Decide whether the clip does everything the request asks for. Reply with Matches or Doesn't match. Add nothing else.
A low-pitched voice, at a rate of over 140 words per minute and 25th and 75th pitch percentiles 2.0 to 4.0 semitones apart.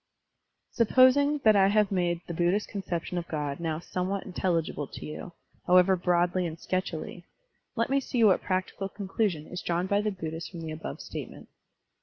Doesn't match